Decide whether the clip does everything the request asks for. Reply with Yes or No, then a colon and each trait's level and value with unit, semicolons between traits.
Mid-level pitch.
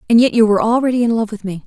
No: high, 225 Hz